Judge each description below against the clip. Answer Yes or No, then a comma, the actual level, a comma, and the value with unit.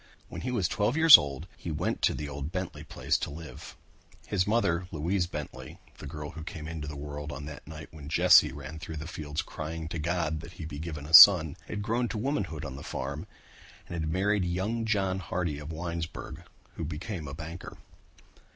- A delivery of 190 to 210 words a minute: Yes, fast, 205 wpm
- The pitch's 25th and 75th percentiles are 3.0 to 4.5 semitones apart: Yes, average, 3.6 semitones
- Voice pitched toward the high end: No, very low, 80 Hz